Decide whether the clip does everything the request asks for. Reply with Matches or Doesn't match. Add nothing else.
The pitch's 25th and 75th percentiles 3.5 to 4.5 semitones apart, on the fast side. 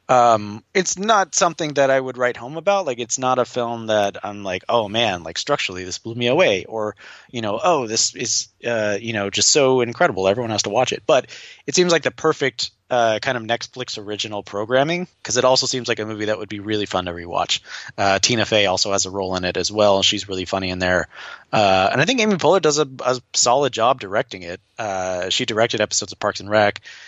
Matches